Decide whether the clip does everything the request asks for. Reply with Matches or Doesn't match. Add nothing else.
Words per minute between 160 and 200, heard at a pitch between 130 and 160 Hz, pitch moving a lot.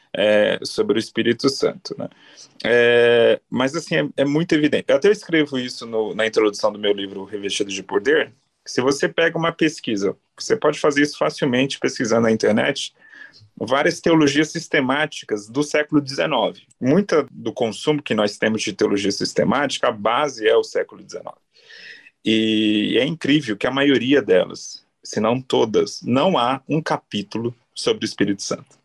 Matches